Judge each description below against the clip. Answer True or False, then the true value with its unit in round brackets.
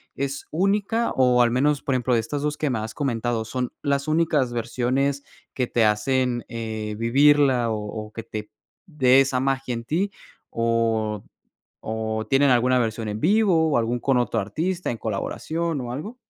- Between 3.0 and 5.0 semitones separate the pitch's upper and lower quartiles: True (4.1 semitones)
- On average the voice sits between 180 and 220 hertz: False (125 Hz)